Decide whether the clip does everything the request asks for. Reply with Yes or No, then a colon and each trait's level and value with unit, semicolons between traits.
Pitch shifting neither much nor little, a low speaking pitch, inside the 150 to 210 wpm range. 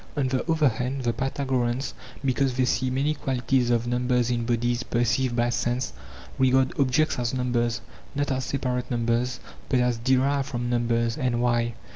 No: narrow, 1.7 semitones; low, 125 Hz; average, 170 wpm